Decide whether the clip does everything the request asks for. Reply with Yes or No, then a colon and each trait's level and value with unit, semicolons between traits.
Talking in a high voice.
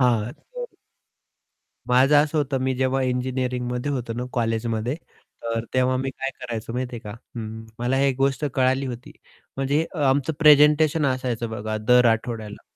No: low, 125 Hz